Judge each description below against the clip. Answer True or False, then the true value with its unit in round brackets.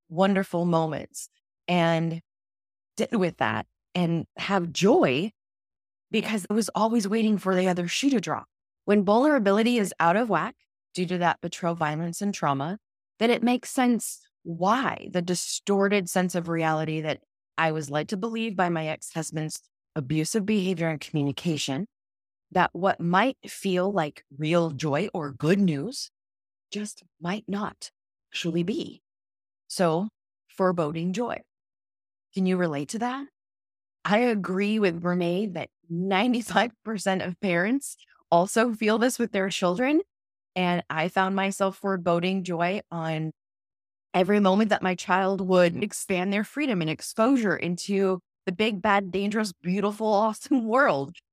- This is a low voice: False (185 Hz)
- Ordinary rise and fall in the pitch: True (4.0 semitones)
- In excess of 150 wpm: False (140 wpm)